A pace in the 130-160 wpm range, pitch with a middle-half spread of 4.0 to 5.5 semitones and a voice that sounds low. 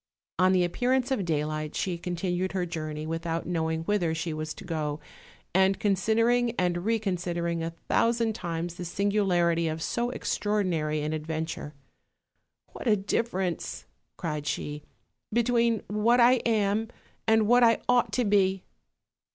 No: average, 145 wpm; average, 5.1 semitones; medium, 185 Hz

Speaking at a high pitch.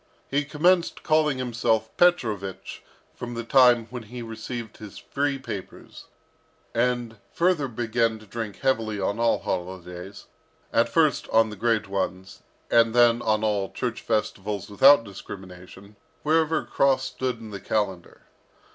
No: low, 115 Hz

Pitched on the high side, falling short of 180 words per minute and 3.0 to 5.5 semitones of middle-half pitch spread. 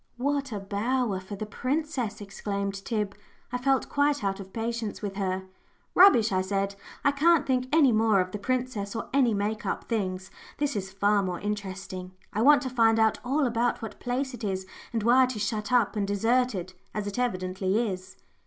No: high, 215 Hz; average, 195 wpm; average, 4.2 semitones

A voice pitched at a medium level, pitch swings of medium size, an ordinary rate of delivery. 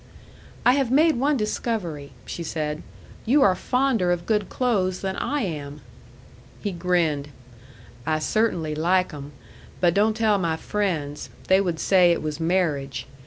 No: medium, 180 Hz; wide, 5.7 semitones; average, 150 wpm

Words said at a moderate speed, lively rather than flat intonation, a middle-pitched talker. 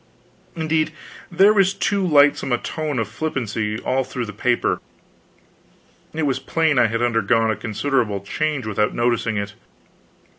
No: average, 145 wpm; wide, 5.8 semitones; low, 125 Hz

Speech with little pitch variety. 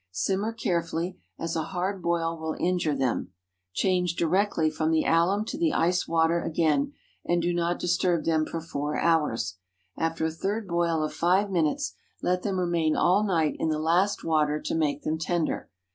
Yes: narrow, 2.2 semitones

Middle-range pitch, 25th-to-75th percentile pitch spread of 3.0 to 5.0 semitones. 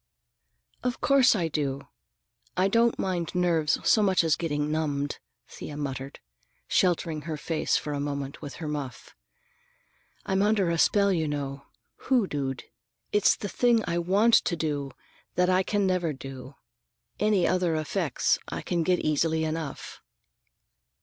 Yes: medium, 165 Hz; average, 4.4 semitones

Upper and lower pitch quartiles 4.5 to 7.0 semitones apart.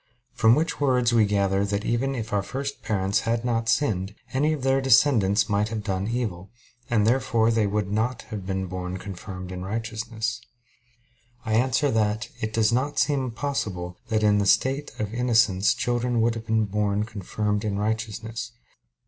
No: average, 3.1 semitones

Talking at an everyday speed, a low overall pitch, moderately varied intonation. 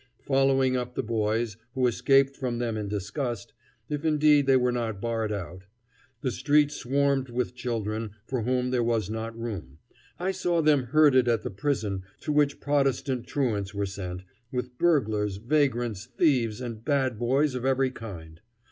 Yes: average, 165 wpm; low, 125 Hz; average, 4.0 semitones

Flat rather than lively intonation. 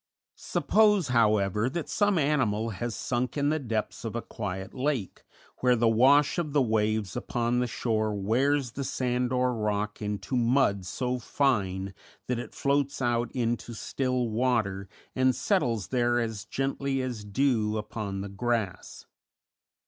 No: average, 3.6 semitones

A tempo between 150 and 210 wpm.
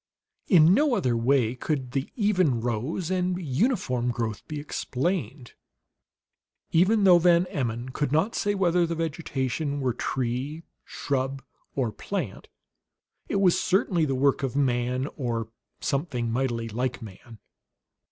No: slow, 135 wpm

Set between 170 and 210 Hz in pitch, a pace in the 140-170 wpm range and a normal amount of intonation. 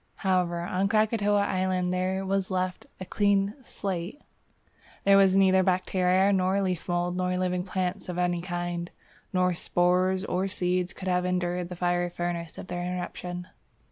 No: medium, 185 Hz; average, 155 wpm; narrow, 1.1 semitones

